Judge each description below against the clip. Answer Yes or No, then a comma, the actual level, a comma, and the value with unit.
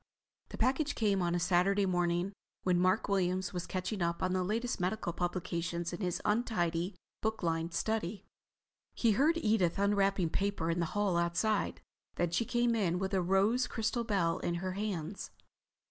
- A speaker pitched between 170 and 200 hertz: Yes, medium, 185 Hz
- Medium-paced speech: Yes, average, 170 wpm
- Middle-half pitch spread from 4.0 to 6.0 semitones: No, average, 3.5 semitones